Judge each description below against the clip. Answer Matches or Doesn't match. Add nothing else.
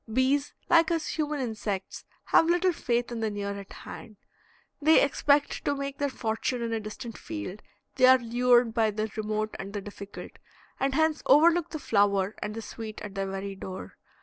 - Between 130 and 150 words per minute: Doesn't match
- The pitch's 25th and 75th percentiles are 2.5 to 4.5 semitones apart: Doesn't match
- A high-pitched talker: Matches